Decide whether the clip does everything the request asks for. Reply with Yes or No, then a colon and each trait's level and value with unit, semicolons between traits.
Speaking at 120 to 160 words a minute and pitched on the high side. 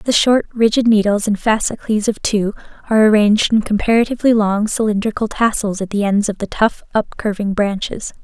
No: average, 175 wpm; high, 215 Hz